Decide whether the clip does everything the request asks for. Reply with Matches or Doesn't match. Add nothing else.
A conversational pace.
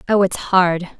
Matches